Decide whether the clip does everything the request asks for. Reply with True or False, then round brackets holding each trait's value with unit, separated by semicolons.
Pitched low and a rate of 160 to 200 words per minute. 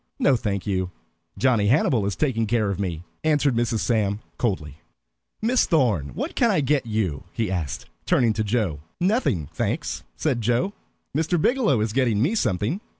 True (115 Hz; 165 wpm)